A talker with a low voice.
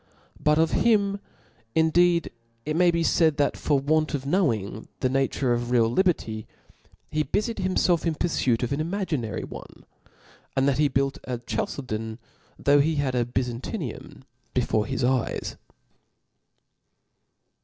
No: medium, 145 Hz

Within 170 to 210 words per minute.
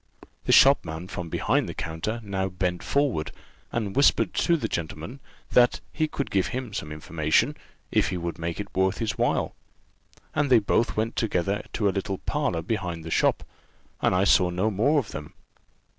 Yes: average, 175 wpm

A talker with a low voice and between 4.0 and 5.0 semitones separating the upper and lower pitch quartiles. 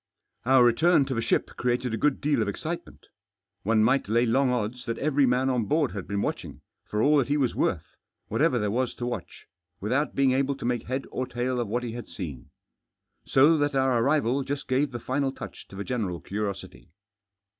No: low, 125 Hz; average, 3.3 semitones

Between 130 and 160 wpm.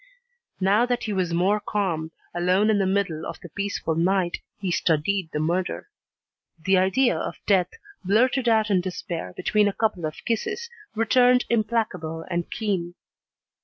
Yes: average, 155 wpm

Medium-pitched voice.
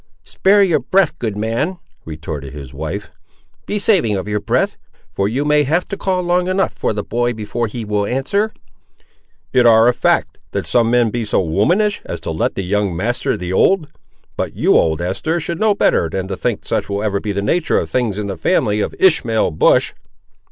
No: low, 115 Hz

